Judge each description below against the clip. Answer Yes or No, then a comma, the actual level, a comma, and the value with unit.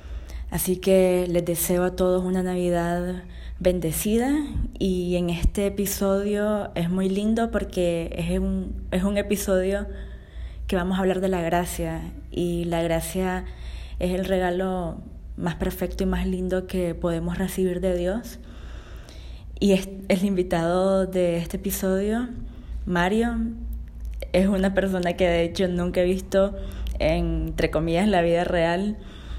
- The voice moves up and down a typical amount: No, narrow, 1.8 semitones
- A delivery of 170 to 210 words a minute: No, average, 140 wpm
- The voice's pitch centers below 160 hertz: No, medium, 185 Hz